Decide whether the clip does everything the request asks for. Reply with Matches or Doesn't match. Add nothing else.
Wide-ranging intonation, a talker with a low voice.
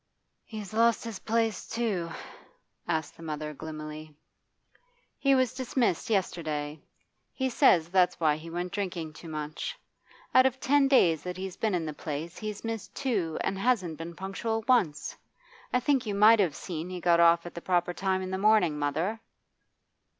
Doesn't match